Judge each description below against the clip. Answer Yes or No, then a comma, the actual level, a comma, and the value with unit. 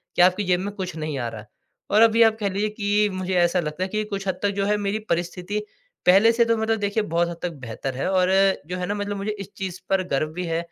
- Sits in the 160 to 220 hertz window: Yes, high, 190 Hz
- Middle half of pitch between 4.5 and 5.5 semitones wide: No, average, 2.9 semitones